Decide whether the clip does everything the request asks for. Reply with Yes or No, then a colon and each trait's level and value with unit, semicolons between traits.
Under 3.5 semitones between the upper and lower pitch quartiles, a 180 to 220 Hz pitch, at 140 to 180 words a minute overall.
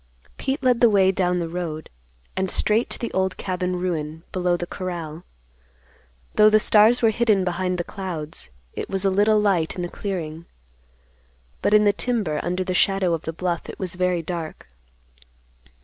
Yes: average, 2.9 semitones; medium, 185 Hz; average, 175 wpm